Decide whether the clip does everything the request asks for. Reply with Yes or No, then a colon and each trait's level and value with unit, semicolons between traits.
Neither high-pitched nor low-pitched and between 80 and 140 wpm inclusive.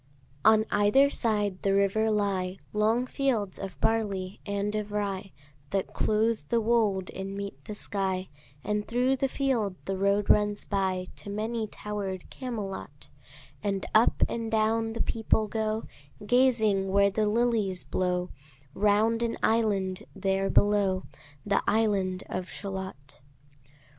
No: high, 205 Hz; slow, 135 wpm